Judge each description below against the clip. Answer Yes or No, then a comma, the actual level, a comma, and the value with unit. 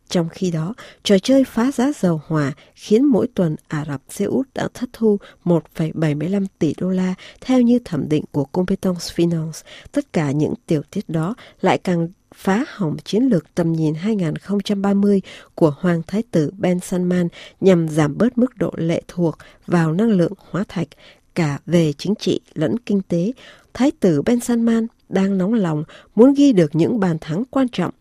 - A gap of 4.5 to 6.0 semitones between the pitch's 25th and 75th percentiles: Yes, average, 5.0 semitones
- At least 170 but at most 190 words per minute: Yes, average, 180 wpm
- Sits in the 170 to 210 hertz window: Yes, medium, 185 Hz